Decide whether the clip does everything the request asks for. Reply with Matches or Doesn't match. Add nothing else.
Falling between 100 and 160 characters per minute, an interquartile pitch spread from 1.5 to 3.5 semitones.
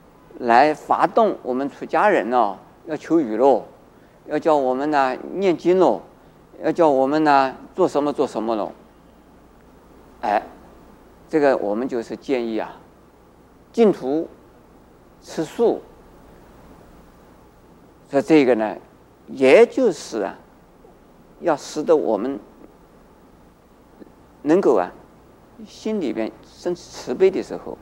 Doesn't match